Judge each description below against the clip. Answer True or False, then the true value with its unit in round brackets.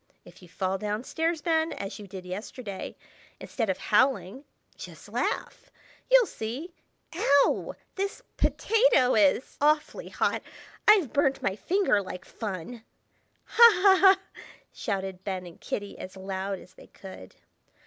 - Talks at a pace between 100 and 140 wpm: True (135 wpm)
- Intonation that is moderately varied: False (8.9 semitones)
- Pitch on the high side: True (220 Hz)